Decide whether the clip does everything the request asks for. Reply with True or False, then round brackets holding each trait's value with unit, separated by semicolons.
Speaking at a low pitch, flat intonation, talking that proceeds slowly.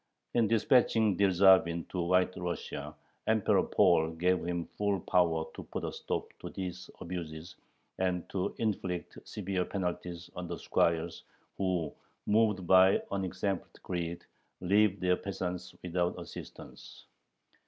True (90 Hz; 2.1 semitones; 125 wpm)